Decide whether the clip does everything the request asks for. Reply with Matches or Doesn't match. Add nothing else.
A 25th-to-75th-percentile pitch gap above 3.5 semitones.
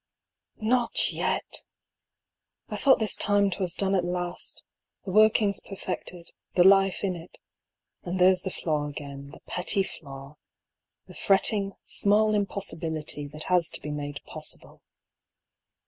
Matches